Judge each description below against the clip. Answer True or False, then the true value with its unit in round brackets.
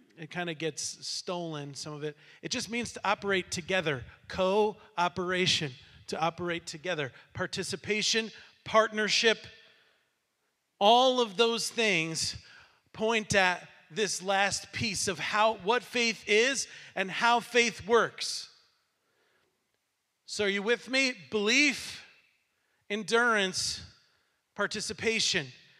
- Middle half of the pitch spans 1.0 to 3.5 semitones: False (4.3 semitones)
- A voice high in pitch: True (200 Hz)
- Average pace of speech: False (105 wpm)